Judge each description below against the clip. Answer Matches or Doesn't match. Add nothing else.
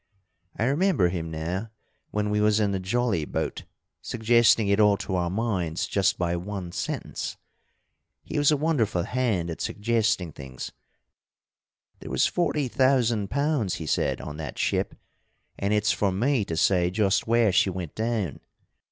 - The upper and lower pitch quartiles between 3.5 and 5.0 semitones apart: Matches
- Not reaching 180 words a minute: Matches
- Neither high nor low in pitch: Doesn't match